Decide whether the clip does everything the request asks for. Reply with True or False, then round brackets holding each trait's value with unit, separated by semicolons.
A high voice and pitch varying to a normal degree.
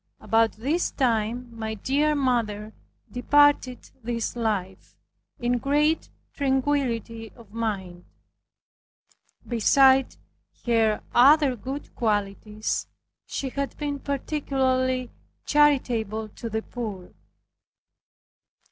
True (245 Hz; 3.8 semitones)